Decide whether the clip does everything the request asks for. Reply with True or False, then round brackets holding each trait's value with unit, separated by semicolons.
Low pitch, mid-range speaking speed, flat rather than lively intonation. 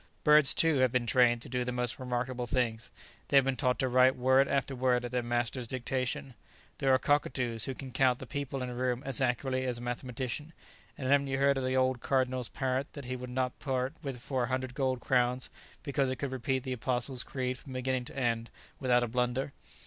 False (130 Hz; 225 wpm; 1.3 semitones)